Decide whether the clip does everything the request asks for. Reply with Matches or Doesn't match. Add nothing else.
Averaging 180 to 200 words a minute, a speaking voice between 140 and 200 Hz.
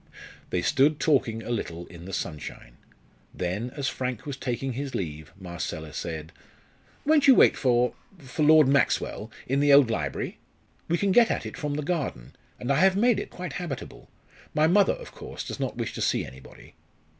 Doesn't match